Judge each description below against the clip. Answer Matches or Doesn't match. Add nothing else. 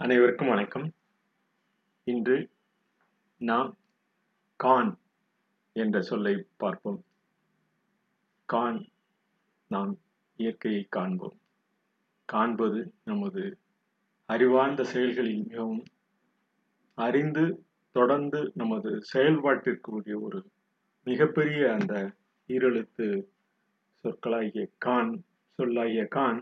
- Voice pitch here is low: Doesn't match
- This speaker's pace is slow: Matches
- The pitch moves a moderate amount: Doesn't match